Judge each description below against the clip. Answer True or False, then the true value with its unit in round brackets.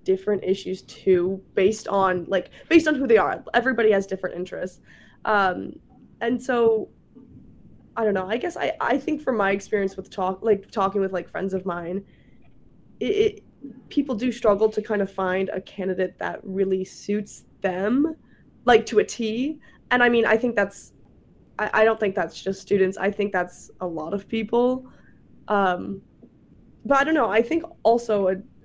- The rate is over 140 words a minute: True (180 wpm)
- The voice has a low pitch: False (205 Hz)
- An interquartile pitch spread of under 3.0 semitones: False (3.8 semitones)